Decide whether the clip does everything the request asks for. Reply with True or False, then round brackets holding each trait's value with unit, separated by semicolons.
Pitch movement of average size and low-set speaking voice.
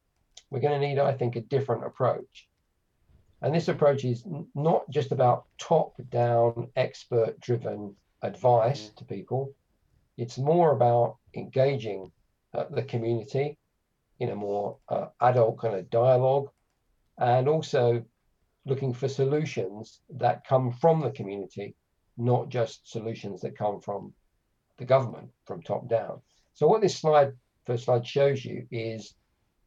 True (3.3 semitones; 125 Hz)